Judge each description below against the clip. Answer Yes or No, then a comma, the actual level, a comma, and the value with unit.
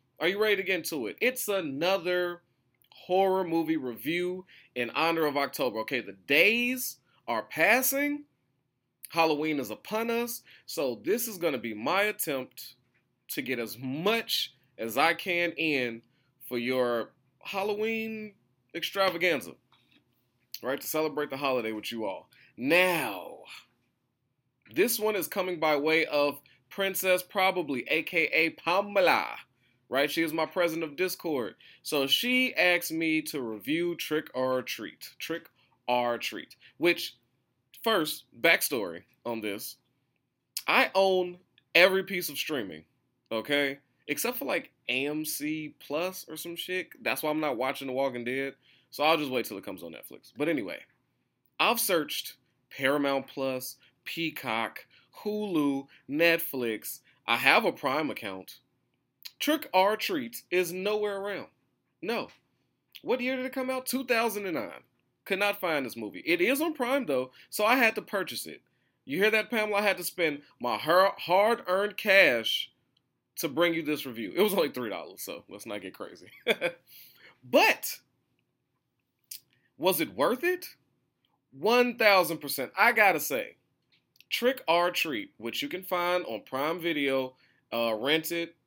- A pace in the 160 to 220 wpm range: No, average, 150 wpm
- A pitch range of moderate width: No, wide, 6.9 semitones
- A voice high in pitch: No, medium, 165 Hz